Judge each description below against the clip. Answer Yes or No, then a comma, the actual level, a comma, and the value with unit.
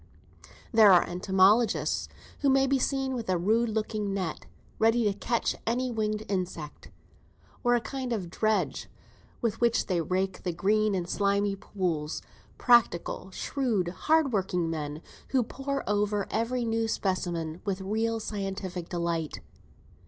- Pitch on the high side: Yes, high, 205 Hz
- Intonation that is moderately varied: Yes, average, 4.0 semitones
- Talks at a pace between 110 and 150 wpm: Yes, average, 140 wpm